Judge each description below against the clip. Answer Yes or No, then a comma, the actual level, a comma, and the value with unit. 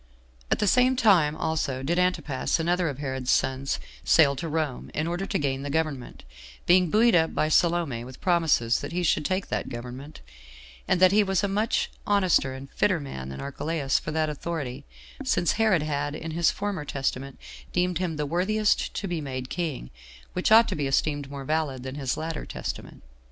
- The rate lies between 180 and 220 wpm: Yes, average, 195 wpm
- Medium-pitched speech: Yes, medium, 155 Hz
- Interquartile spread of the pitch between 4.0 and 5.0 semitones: Yes, average, 4.6 semitones